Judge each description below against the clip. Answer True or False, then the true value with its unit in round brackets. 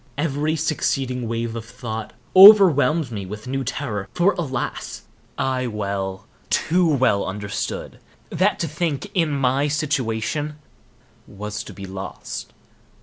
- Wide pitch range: True (6.1 semitones)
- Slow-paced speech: True (125 wpm)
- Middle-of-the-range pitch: False (130 Hz)